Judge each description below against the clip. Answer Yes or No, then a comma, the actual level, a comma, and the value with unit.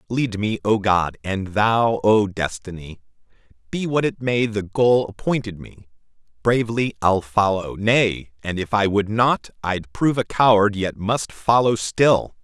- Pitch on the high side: No, low, 105 Hz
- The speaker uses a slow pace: No, average, 160 wpm